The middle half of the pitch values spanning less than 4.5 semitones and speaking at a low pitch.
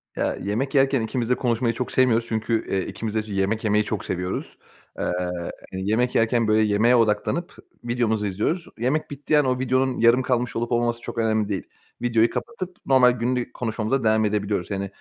Yes: average, 2.7 semitones; low, 115 Hz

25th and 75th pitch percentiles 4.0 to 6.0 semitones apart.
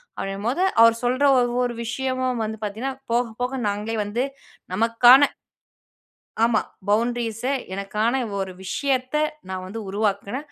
No: average, 3.3 semitones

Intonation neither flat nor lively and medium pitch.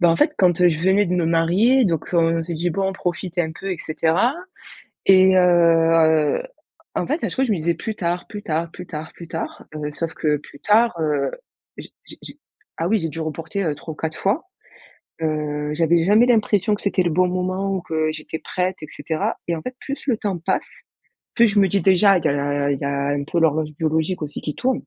Yes: average, 3.4 semitones; medium, 170 Hz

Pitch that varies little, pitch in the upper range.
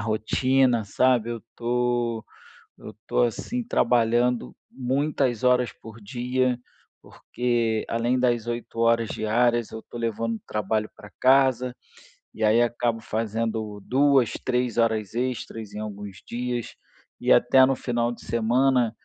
No: narrow, 2.0 semitones; low, 120 Hz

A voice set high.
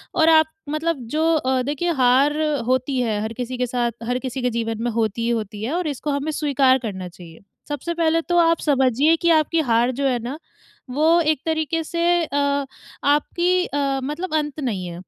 Yes: very high, 275 Hz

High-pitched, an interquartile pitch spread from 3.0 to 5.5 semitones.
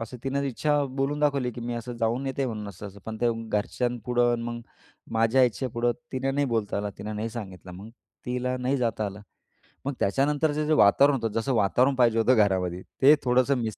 No: low, 120 Hz; average, 3.6 semitones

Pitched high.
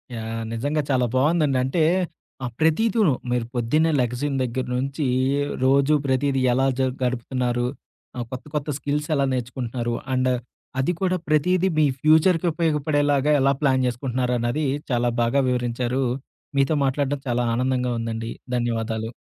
No: low, 130 Hz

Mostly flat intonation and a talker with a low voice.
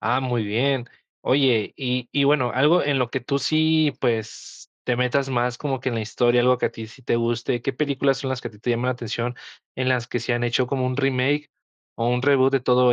Yes: narrow, 2.1 semitones; low, 125 Hz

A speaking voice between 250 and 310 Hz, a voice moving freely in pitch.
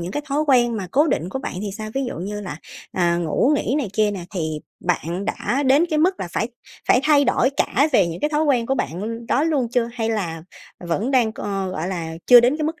No: high, 230 Hz; wide, 6.8 semitones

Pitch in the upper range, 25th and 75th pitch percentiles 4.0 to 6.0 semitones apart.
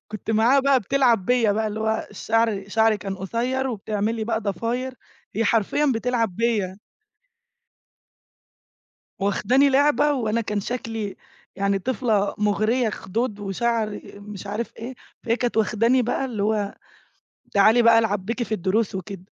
No: high, 220 Hz; average, 2.8 semitones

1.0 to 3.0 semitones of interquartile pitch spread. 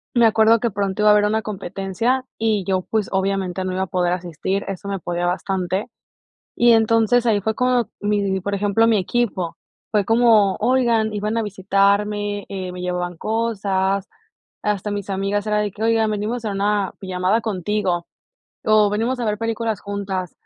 Yes: narrow, 2.5 semitones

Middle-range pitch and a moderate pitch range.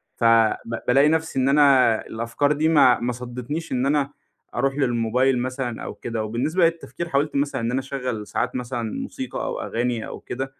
No: low, 130 Hz; average, 3.2 semitones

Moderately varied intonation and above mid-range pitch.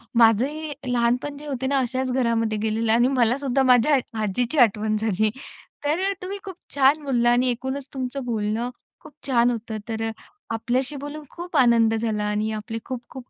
Yes: average, 3.5 semitones; high, 245 Hz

